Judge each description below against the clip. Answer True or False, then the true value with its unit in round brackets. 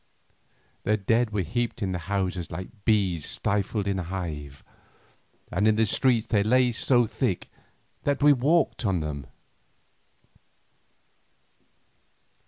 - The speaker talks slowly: True (125 wpm)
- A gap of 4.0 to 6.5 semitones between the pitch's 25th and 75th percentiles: True (4.6 semitones)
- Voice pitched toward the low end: True (105 Hz)